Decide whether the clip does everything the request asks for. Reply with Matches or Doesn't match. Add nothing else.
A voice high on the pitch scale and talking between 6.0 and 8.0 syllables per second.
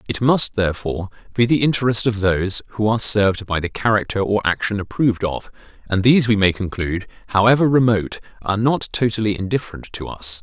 Doesn't match